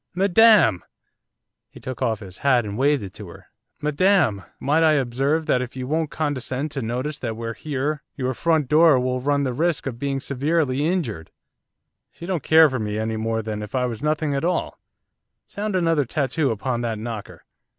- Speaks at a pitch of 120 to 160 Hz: Yes, low, 135 Hz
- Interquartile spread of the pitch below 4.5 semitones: No, average, 4.8 semitones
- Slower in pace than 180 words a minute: No, average, 190 wpm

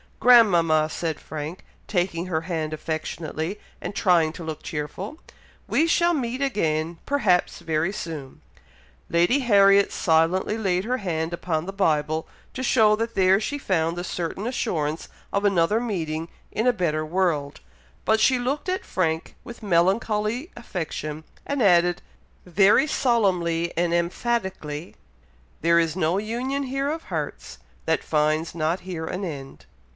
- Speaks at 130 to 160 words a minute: Yes, average, 140 wpm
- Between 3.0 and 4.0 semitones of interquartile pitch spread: No, average, 5.3 semitones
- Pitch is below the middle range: No, medium, 180 Hz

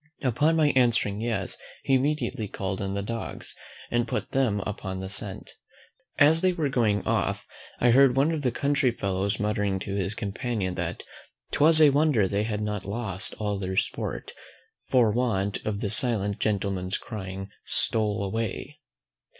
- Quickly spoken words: No, average, 160 wpm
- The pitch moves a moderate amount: Yes, average, 4.5 semitones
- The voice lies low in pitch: Yes, low, 110 Hz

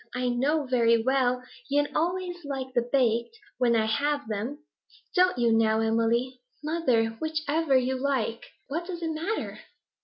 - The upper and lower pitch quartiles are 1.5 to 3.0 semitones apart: No, average, 4.8 semitones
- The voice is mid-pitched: No, very high, 260 Hz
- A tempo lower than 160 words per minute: Yes, average, 150 wpm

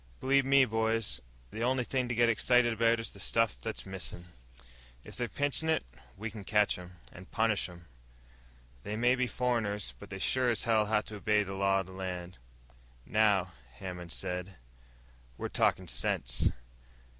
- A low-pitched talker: Yes, low, 110 Hz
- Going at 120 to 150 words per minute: No, average, 170 wpm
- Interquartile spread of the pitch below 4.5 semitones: Yes, average, 3.7 semitones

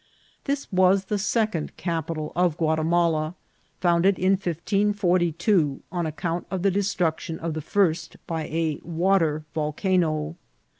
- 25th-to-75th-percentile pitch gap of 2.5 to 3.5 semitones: Yes, average, 3.1 semitones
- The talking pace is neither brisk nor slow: No, slow, 120 wpm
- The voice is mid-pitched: Yes, medium, 170 Hz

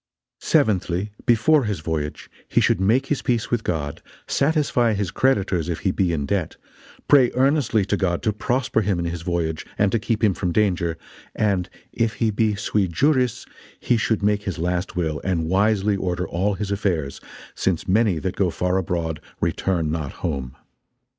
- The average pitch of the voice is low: Yes, very low, 95 Hz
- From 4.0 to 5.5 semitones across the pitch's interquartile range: Yes, average, 4.3 semitones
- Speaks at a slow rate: No, average, 175 wpm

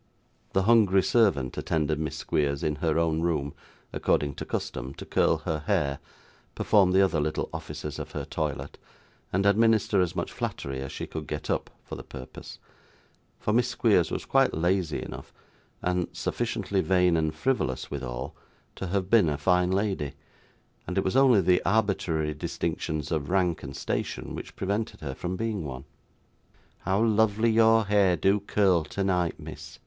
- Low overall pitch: Yes, very low, 90 Hz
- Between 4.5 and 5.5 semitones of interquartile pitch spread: Yes, average, 4.8 semitones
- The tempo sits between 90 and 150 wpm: No, average, 165 wpm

